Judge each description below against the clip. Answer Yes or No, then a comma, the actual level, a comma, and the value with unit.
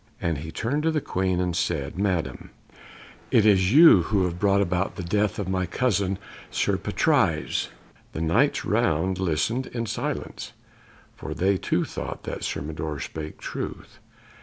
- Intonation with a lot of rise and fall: No, average, 3.6 semitones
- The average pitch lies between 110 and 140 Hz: No, very low, 95 Hz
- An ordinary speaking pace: Yes, average, 155 wpm